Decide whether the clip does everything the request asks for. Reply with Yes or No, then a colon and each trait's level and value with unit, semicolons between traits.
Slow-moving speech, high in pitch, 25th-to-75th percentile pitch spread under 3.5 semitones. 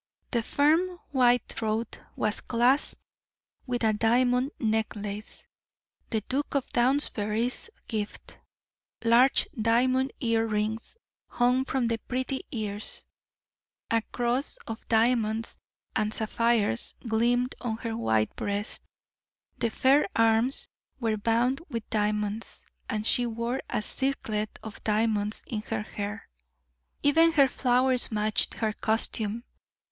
Yes: slow, 115 wpm; high, 230 Hz; narrow, 2.6 semitones